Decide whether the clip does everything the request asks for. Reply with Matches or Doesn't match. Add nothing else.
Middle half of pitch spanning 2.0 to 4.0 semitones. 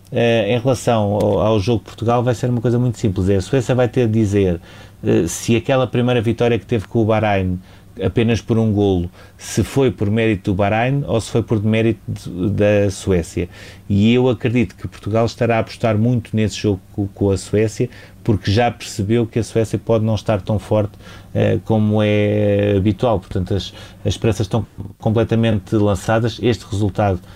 Matches